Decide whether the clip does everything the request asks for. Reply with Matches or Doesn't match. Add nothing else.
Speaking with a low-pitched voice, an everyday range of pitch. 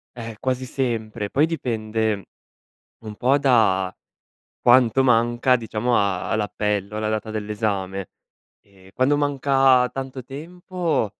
Matches